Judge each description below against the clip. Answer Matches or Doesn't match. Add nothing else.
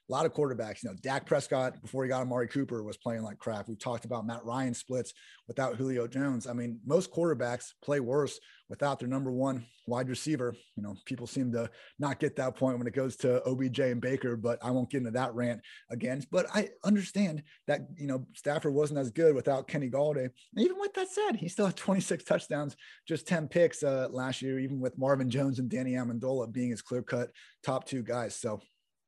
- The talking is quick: Matches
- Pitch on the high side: Doesn't match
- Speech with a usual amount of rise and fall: Matches